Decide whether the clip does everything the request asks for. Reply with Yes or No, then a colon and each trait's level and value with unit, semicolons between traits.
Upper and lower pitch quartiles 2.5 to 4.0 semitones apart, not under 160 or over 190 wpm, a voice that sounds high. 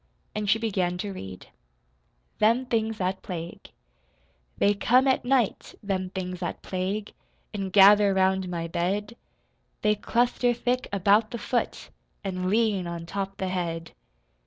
No: average, 3.0 semitones; average, 140 wpm; high, 195 Hz